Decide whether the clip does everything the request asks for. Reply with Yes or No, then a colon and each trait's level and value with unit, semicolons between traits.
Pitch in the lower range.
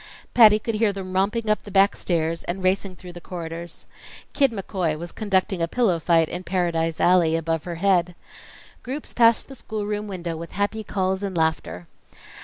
No: medium, 185 Hz